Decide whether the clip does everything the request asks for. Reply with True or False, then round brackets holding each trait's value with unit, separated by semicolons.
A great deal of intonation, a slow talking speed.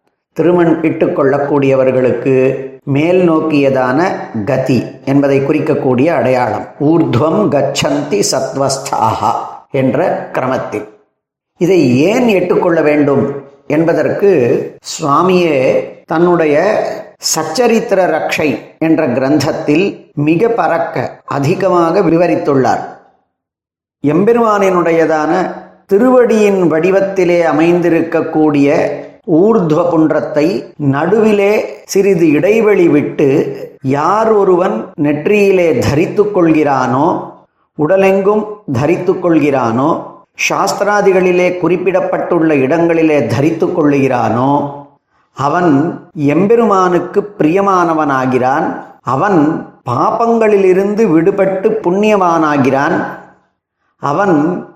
False (5.0 semitones; 60 wpm)